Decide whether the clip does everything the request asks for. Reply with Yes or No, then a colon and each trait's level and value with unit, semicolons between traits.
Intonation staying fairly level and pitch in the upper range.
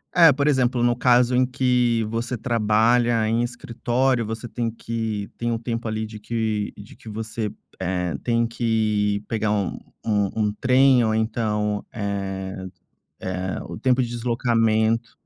No: narrow, 2.2 semitones; low, 115 Hz